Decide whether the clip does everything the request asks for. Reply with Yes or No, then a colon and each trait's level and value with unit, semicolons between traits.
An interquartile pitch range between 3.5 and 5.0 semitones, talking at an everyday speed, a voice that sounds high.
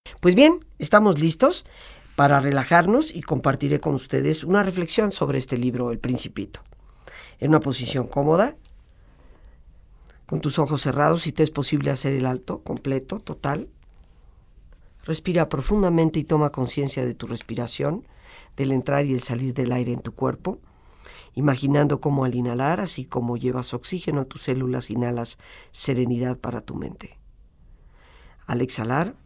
No: average, 4.0 semitones; average, 145 wpm; low, 135 Hz